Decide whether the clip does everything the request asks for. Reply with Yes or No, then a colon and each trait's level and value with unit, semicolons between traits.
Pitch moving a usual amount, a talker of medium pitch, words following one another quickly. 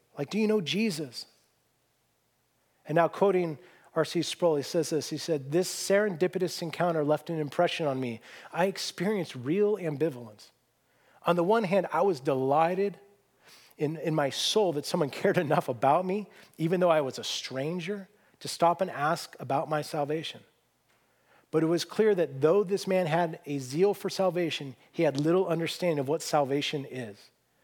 No: average, 3.9 semitones; medium, 165 Hz; average, 170 wpm